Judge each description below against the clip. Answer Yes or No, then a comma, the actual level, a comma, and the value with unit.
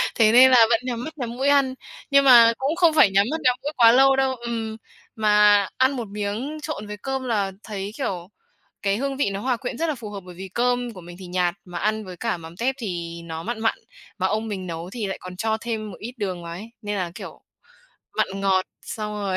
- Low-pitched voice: No, high, 220 Hz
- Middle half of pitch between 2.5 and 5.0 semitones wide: Yes, average, 4.6 semitones